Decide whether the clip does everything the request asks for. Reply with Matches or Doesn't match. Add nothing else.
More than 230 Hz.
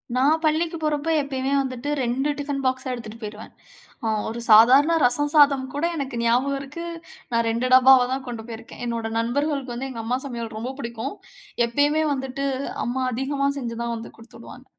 Matches